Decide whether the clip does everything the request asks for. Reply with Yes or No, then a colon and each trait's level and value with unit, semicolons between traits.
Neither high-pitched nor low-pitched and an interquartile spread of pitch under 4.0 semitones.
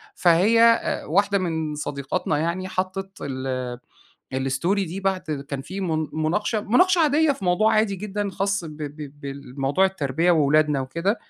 No: medium, 175 Hz; average, 5.2 semitones